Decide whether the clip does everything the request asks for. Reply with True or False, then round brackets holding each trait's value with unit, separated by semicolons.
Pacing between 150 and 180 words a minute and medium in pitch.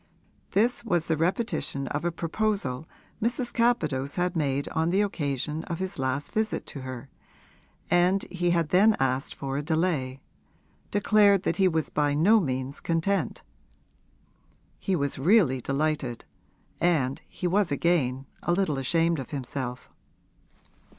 False (140 wpm; 160 Hz)